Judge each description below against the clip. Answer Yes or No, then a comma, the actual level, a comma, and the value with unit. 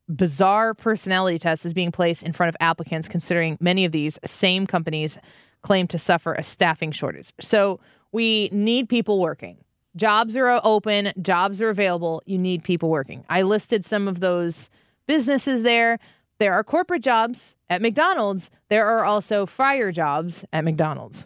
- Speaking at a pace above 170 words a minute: No, average, 160 wpm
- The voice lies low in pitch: No, medium, 185 Hz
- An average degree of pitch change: Yes, average, 4.6 semitones